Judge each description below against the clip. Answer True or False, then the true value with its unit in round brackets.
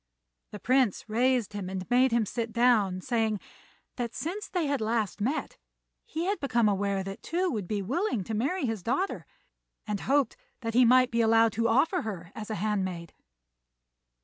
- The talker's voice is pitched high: True (230 Hz)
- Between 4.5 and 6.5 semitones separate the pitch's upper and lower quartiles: False (3.9 semitones)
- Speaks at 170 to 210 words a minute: True (175 wpm)